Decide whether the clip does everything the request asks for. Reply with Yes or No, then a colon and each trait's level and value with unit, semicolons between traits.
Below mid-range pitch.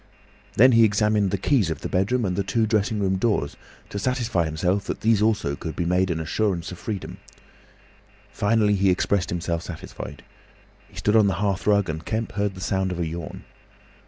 Yes: low, 100 Hz